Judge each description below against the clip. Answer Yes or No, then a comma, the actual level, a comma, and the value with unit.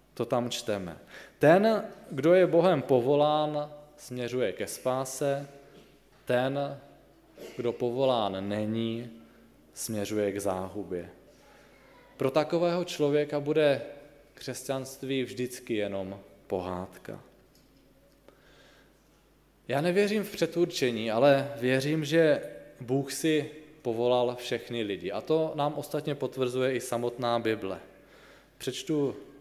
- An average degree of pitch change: Yes, average, 4.2 semitones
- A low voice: Yes, low, 130 Hz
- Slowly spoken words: Yes, slow, 95 wpm